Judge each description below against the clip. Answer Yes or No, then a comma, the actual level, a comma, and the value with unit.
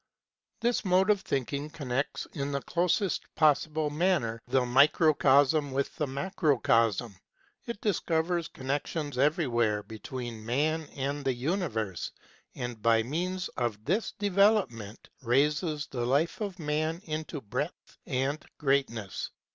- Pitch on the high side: No, medium, 145 Hz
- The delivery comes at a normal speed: No, slow, 125 wpm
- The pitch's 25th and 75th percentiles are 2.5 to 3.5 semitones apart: No, average, 5.0 semitones